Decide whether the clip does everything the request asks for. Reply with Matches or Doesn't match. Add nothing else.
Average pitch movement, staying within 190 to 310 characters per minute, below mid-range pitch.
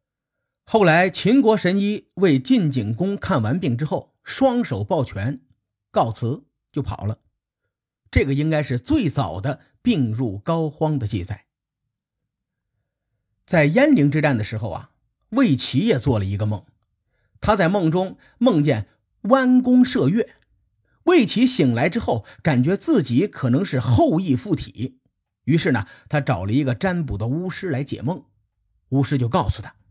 Doesn't match